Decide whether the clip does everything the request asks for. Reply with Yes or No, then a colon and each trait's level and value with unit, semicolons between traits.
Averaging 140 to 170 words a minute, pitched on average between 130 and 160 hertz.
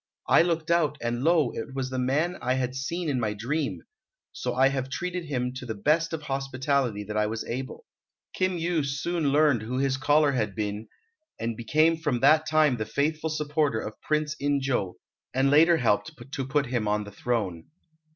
No: average, 195 wpm; low, 135 Hz